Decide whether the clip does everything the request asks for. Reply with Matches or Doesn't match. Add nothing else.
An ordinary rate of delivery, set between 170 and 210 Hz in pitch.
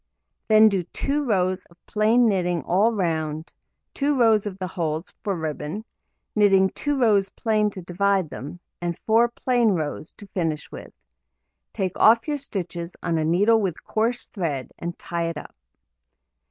Matches